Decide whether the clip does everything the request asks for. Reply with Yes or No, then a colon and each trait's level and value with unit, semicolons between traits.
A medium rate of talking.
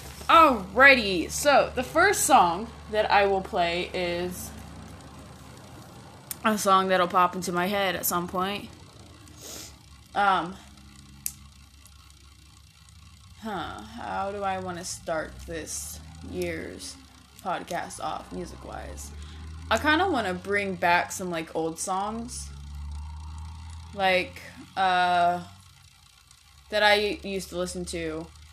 No: slow, 110 wpm